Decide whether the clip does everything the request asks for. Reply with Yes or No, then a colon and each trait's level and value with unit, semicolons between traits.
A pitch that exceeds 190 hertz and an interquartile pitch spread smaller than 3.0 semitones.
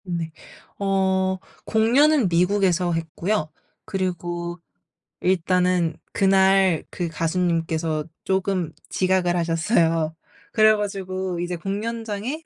No: medium, 185 Hz; narrow, 2.5 semitones